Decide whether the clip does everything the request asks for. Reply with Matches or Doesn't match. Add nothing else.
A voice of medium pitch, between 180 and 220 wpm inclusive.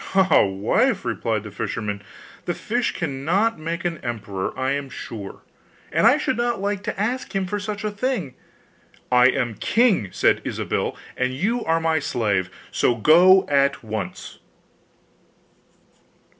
Doesn't match